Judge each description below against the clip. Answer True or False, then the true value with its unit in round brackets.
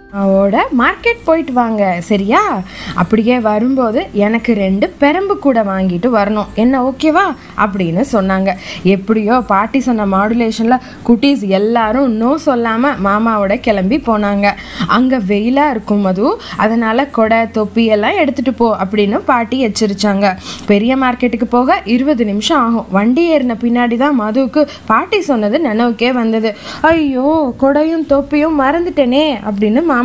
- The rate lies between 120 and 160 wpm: True (125 wpm)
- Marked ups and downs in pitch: False (4.8 semitones)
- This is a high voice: True (235 Hz)